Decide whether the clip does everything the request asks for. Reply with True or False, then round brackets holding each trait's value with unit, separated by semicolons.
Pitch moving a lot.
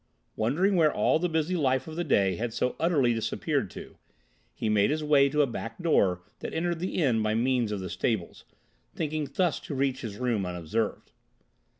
True (6.2 semitones)